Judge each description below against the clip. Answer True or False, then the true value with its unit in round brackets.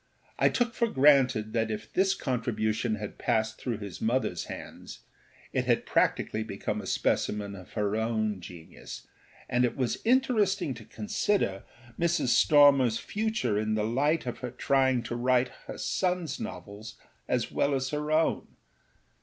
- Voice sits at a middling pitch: False (125 Hz)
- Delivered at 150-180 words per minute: True (155 wpm)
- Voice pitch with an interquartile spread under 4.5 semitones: False (5.4 semitones)